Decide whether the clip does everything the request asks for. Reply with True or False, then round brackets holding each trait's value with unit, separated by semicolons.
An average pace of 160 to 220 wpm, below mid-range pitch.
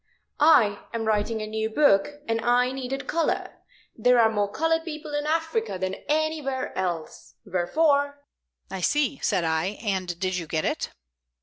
False (165 wpm; 230 Hz)